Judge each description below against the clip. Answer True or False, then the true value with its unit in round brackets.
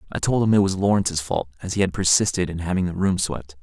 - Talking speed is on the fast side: True (265 wpm)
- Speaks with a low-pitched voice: True (90 Hz)